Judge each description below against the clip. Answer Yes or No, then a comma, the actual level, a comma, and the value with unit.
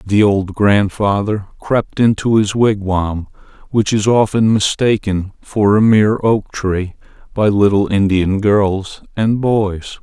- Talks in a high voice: No, low, 105 Hz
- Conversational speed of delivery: No, slow, 130 wpm